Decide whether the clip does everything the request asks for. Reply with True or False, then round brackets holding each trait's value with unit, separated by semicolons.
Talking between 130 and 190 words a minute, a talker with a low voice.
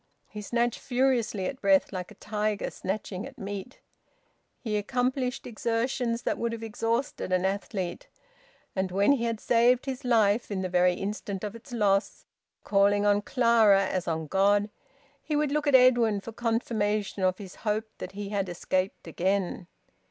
False (165 wpm; 210 Hz)